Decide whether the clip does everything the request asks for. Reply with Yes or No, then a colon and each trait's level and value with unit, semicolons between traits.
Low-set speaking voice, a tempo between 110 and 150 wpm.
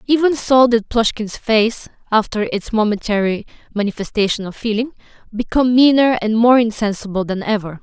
No: high, 225 Hz; average, 140 wpm